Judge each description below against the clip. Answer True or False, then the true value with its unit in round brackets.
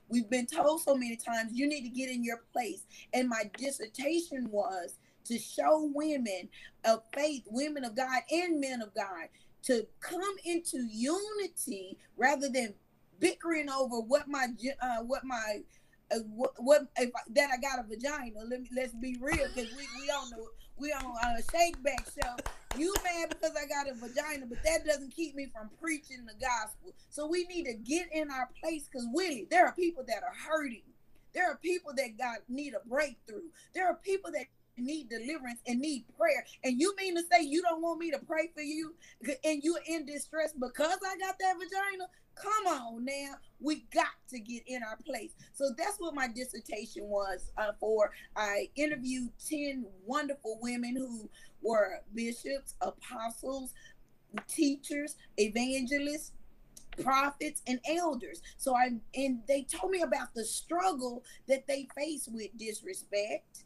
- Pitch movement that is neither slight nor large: True (4.5 semitones)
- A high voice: True (275 Hz)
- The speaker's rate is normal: True (175 wpm)